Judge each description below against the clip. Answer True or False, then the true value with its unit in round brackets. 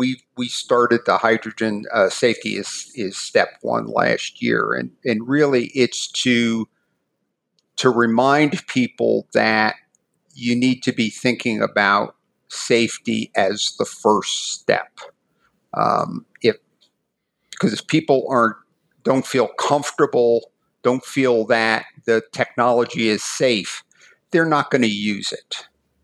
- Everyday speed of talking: False (125 wpm)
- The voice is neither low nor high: False (120 Hz)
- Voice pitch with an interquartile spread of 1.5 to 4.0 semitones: True (2.5 semitones)